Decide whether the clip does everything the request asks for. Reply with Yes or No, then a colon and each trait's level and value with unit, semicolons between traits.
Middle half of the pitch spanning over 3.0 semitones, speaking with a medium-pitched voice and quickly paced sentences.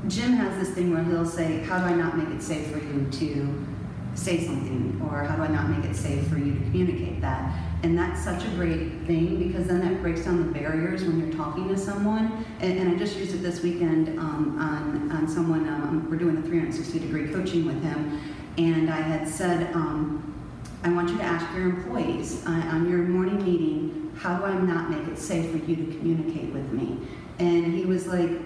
No: narrow, 2.5 semitones; medium, 165 Hz; fast, 220 wpm